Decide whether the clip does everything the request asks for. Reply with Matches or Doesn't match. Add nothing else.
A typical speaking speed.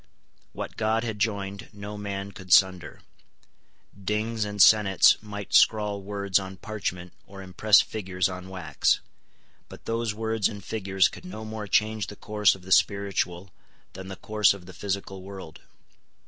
Matches